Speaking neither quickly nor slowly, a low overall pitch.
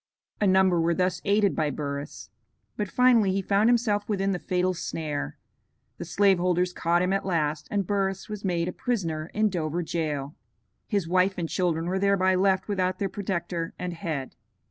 No: average, 180 wpm; medium, 185 Hz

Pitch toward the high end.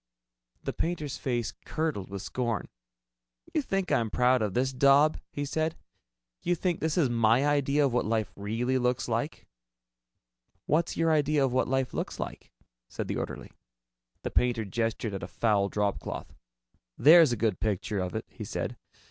No: low, 125 Hz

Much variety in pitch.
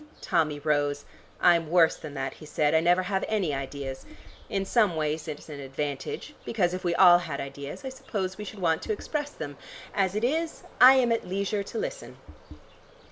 Yes: wide, 6.0 semitones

